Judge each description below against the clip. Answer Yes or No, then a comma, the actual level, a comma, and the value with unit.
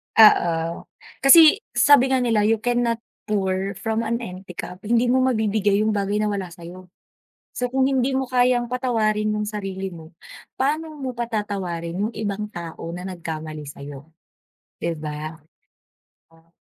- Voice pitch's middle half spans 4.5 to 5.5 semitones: Yes, average, 5.2 semitones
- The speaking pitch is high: Yes, high, 210 Hz